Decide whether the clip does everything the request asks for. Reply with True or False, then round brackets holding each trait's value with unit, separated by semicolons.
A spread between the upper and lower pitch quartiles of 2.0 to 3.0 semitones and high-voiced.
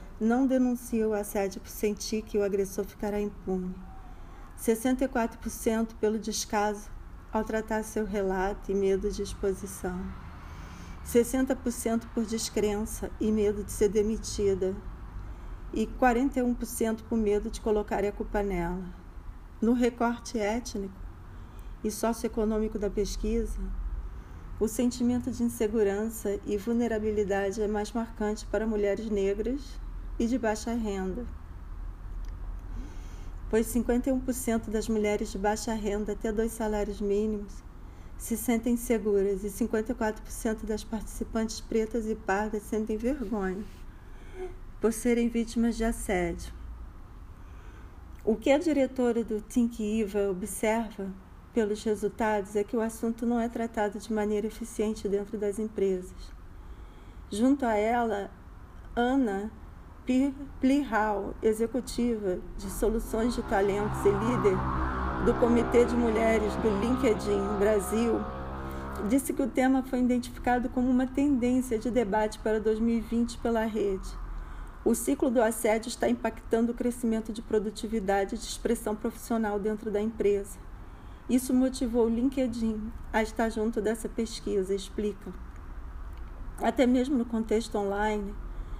True (2.6 semitones; 215 Hz)